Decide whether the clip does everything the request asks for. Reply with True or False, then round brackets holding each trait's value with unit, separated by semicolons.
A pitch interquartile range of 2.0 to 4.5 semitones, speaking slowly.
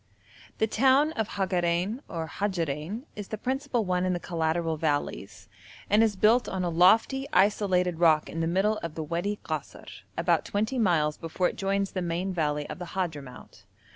False (4.2 semitones; 175 wpm)